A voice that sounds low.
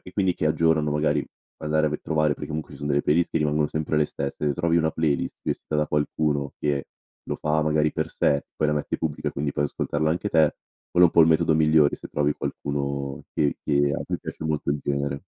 Yes: very low, 75 Hz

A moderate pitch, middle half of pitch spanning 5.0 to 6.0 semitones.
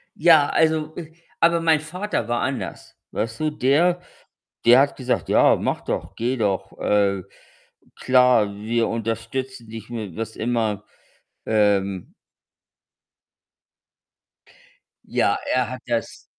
No: low, 120 Hz; wide, 5.5 semitones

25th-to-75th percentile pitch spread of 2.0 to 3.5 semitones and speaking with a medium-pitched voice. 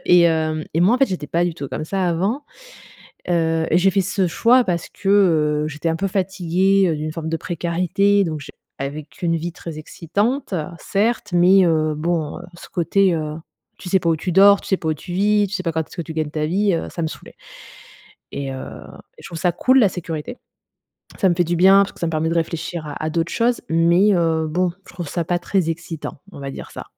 Yes: average, 3.1 semitones; medium, 170 Hz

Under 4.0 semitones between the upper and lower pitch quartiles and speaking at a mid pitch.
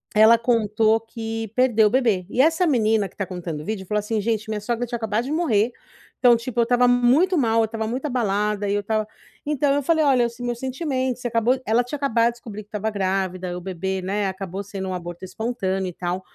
No: average, 3.6 semitones; high, 225 Hz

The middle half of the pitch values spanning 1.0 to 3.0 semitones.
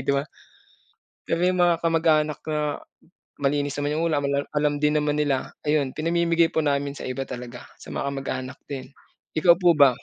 Yes: average, 2.7 semitones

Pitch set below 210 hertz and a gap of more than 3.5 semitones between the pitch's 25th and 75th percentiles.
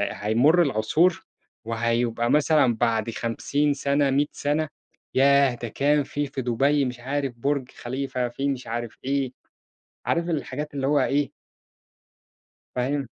No: low, 135 Hz; average, 3.2 semitones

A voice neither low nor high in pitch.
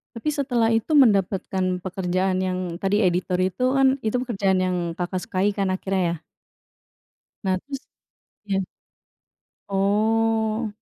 No: high, 195 Hz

